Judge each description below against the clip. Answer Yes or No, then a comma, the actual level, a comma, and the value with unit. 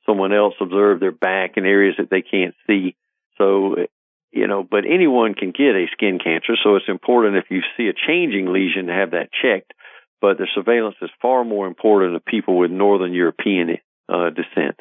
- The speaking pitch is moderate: No, low, 100 Hz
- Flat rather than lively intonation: Yes, narrow, 1.9 semitones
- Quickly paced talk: No, average, 195 wpm